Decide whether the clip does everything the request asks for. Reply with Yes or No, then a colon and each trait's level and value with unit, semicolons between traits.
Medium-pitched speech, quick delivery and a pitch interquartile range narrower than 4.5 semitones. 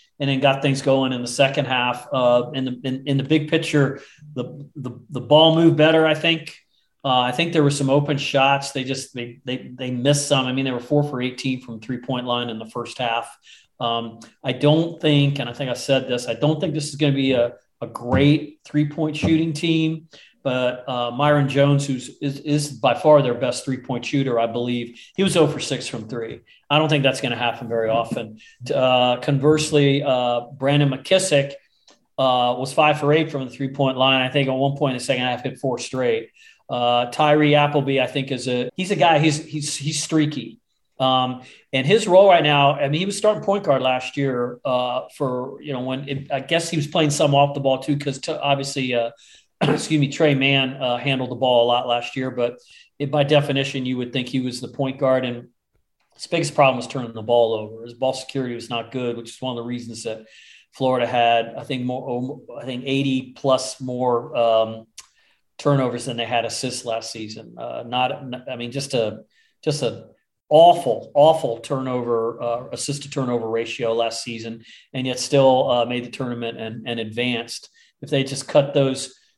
No: low, 130 Hz; fast, 215 wpm; average, 2.9 semitones